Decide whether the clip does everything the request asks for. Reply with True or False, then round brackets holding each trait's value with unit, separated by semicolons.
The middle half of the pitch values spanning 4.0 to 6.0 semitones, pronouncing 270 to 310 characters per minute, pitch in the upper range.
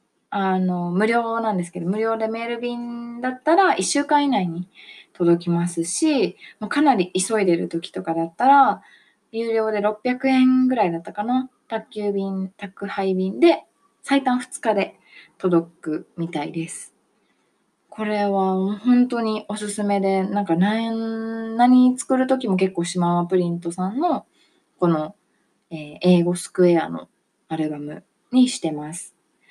False (5.3 semitones; 255 characters per minute; 205 Hz)